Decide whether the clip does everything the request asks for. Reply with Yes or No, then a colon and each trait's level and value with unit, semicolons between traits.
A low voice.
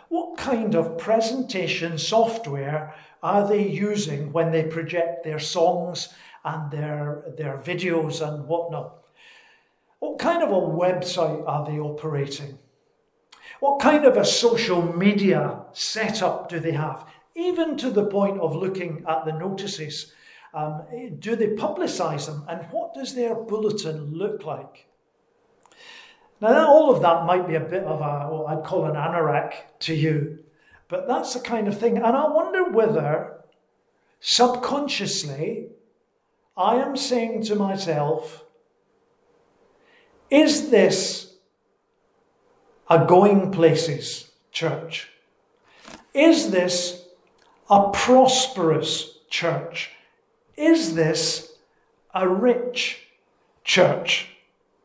No: high, 195 Hz